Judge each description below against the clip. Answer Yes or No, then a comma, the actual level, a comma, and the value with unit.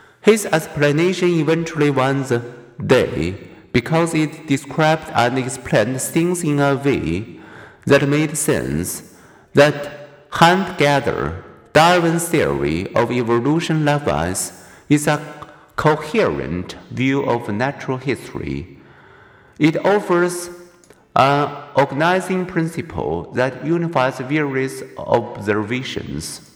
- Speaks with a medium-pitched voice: Yes, medium, 145 Hz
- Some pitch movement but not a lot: Yes, average, 4.4 semitones